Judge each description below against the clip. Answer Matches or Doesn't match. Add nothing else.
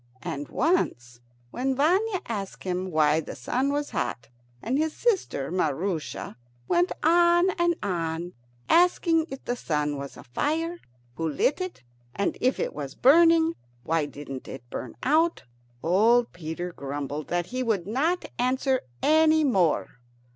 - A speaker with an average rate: Matches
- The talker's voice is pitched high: Matches